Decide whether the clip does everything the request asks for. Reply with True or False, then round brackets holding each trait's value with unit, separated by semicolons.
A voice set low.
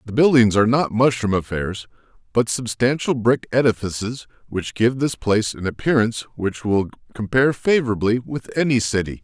True (115 Hz)